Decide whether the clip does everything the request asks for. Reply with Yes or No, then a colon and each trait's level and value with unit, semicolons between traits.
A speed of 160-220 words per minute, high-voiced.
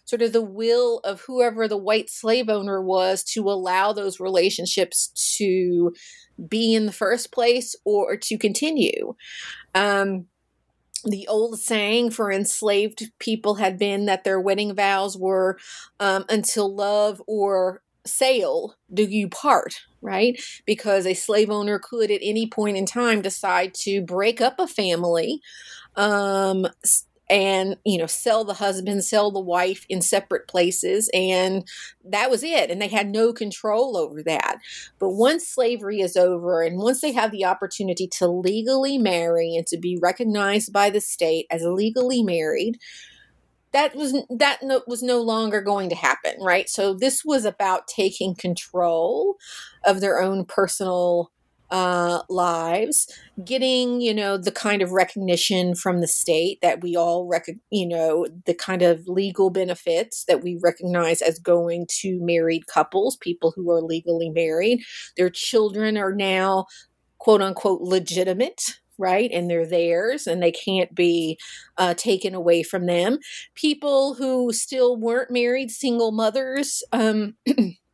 No: average, 150 wpm; high, 200 Hz